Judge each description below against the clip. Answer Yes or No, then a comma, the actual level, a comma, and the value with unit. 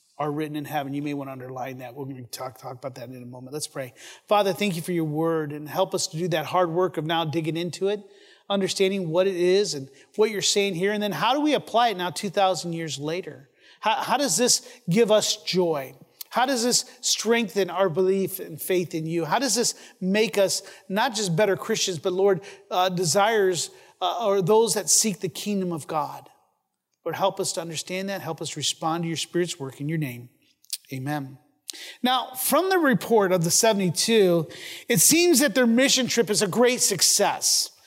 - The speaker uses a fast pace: Yes, fast, 210 wpm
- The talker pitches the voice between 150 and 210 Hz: Yes, medium, 185 Hz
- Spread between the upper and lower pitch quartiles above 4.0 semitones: Yes, average, 4.7 semitones